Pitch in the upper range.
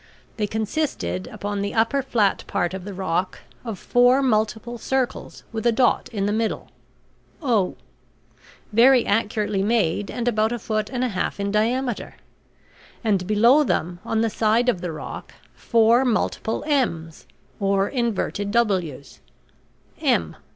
Yes: high, 220 Hz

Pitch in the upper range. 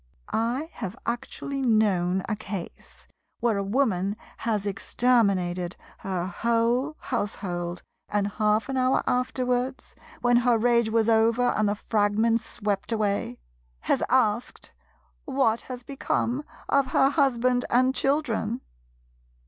Yes: high, 230 Hz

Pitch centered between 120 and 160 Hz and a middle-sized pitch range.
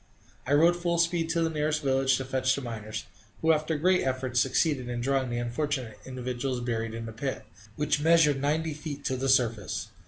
Yes: low, 135 Hz; average, 4.0 semitones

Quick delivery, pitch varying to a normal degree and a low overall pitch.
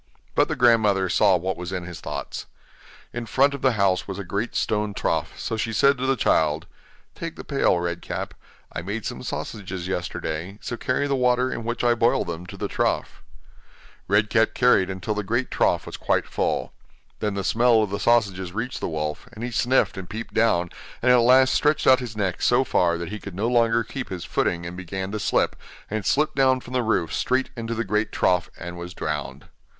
Yes: fast, 215 wpm; average, 4.8 semitones; low, 105 Hz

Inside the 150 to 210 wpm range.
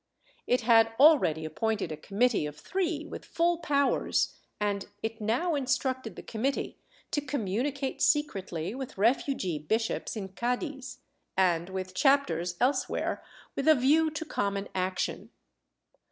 No: slow, 135 wpm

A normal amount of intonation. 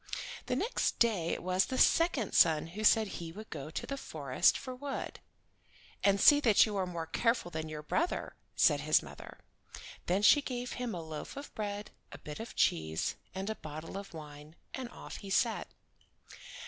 No: wide, 6.8 semitones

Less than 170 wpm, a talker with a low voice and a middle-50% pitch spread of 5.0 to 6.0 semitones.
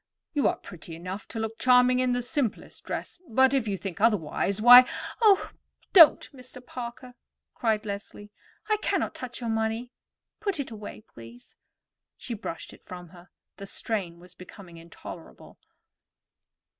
No: average, 150 wpm; high, 225 Hz; average, 5.3 semitones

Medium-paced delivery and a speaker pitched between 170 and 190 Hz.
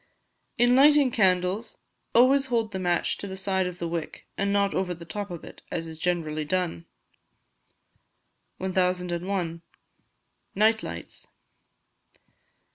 No: slow, 125 wpm; medium, 185 Hz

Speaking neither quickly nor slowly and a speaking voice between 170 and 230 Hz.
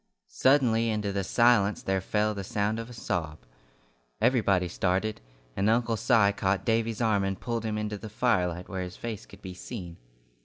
No: average, 180 wpm; low, 105 Hz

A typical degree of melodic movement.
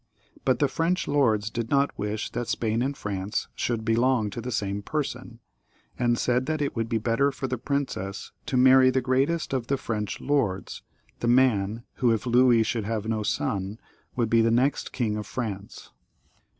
Yes: average, 3.3 semitones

